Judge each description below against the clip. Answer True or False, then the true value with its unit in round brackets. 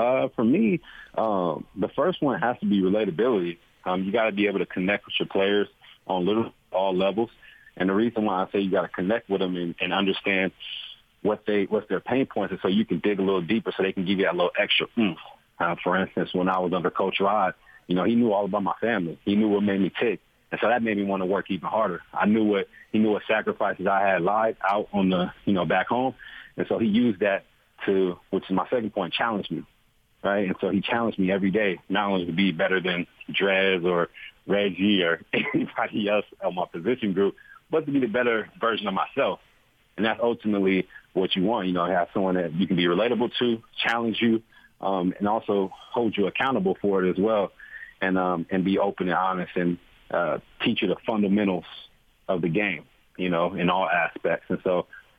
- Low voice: True (95 Hz)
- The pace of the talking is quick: True (230 wpm)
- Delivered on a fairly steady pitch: True (2.0 semitones)